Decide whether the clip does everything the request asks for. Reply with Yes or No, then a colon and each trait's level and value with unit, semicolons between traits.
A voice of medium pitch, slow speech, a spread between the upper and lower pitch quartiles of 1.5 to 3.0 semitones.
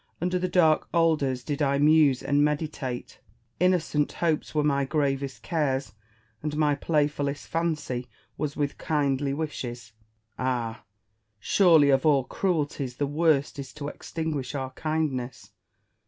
Yes: medium, 145 Hz; slow, 130 wpm; narrow, 2.5 semitones